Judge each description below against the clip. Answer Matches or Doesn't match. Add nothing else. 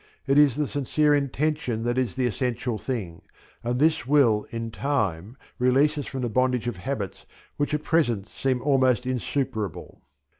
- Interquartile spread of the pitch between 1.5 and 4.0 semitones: Matches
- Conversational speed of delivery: Matches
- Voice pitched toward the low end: Matches